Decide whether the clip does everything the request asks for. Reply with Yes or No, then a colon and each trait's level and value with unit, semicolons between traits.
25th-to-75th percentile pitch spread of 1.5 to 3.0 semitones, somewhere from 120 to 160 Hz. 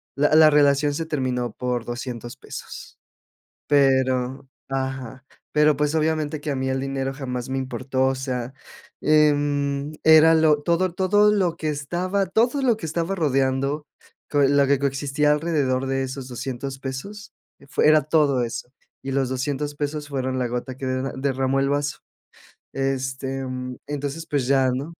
Yes: narrow, 2.4 semitones; medium, 140 Hz